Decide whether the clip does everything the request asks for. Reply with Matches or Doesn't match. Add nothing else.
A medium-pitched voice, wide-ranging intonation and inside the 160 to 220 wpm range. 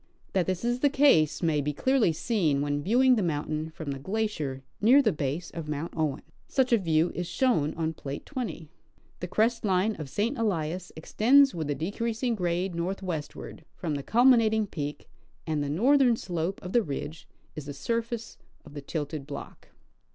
Matches